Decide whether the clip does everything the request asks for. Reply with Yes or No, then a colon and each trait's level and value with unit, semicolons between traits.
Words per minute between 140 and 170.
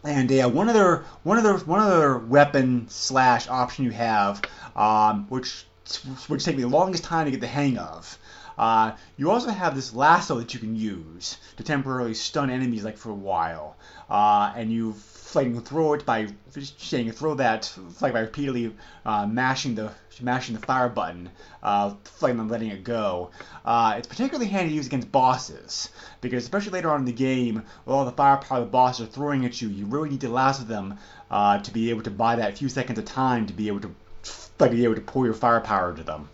No: fast, 205 wpm